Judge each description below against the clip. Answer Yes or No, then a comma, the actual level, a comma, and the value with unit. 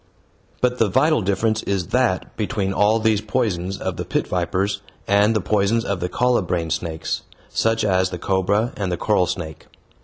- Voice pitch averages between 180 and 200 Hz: No, low, 100 Hz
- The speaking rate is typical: Yes, average, 175 wpm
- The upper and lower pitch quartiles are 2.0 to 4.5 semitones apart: Yes, average, 3.5 semitones